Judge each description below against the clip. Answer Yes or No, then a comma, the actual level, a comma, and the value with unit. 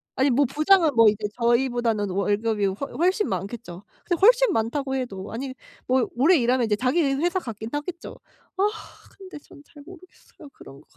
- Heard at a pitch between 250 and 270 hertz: Yes, very high, 260 Hz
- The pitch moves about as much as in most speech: No, wide, 5.7 semitones